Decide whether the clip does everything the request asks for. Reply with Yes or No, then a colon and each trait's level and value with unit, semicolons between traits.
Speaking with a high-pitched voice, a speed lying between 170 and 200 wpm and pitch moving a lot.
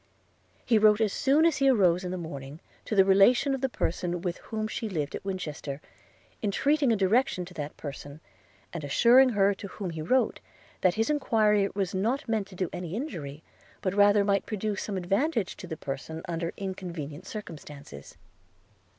No: high, 195 Hz; average, 180 wpm; average, 4.6 semitones